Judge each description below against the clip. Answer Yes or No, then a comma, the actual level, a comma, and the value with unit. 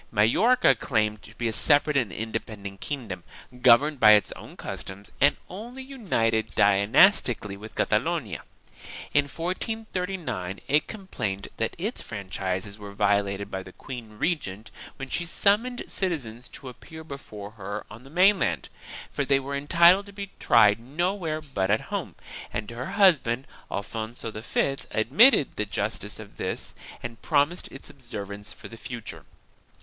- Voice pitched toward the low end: Yes, low, 120 Hz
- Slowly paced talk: No, average, 145 wpm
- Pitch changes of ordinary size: No, wide, 7.8 semitones